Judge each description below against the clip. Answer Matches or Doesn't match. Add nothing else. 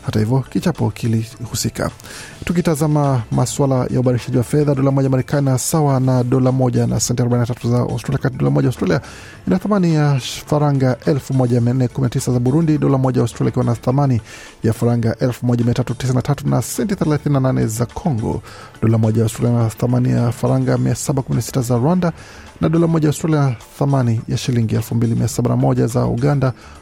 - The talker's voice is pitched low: Matches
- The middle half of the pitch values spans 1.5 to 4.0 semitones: Matches